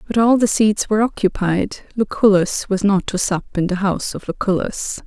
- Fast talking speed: No, average, 190 wpm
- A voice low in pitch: No, high, 200 Hz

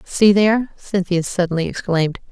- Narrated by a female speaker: Yes, female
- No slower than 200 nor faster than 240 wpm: No, slow, 130 wpm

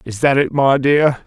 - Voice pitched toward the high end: No, low, 135 Hz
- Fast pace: Yes, fast, 235 wpm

